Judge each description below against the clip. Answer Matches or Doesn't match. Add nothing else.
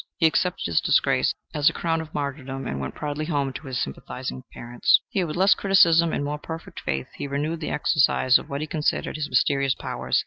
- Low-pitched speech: Doesn't match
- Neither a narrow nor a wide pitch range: Matches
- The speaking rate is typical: Doesn't match